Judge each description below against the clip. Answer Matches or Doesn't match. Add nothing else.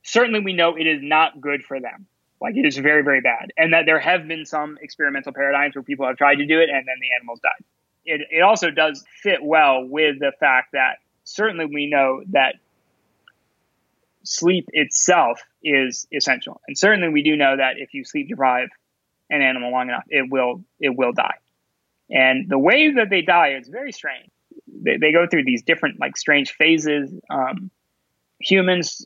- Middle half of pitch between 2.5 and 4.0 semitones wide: Doesn't match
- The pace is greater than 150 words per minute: Matches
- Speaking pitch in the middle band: Matches